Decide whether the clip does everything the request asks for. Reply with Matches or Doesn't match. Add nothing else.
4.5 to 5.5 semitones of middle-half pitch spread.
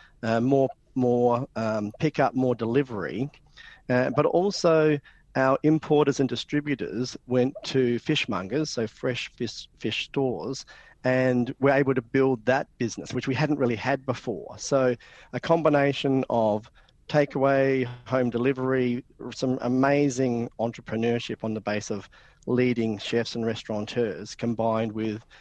Doesn't match